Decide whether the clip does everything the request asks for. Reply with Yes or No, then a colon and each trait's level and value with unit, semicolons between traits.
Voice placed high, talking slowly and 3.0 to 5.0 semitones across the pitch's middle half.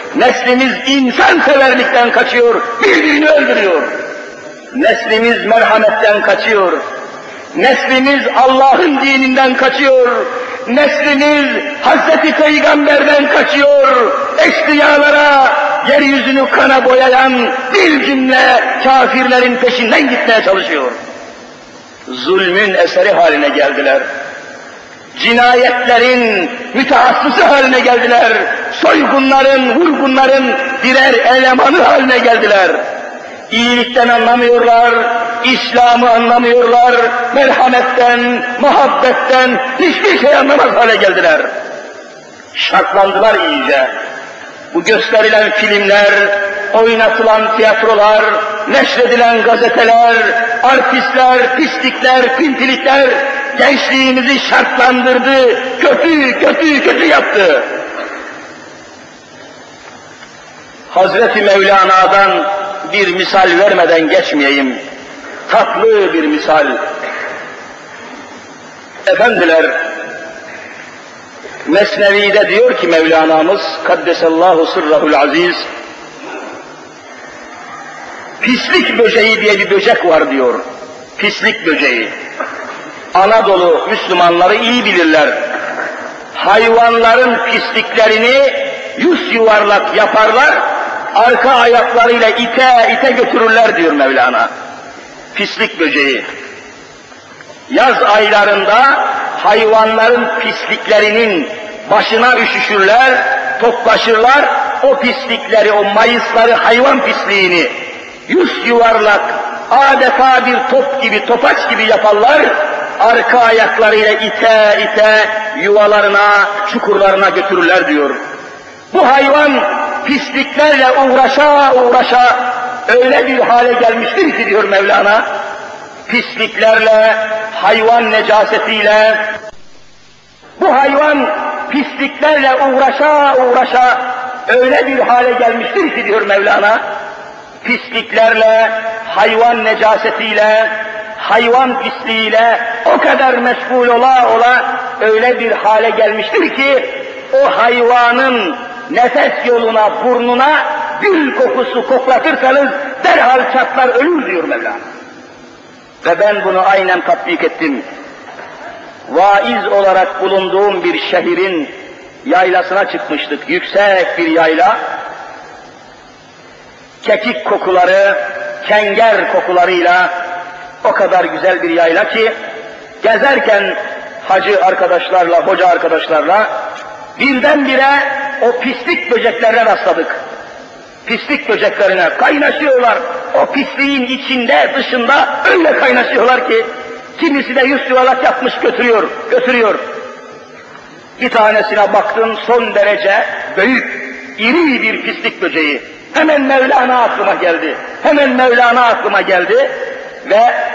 Yes: high, 240 Hz; slow, 80 wpm; average, 4.1 semitones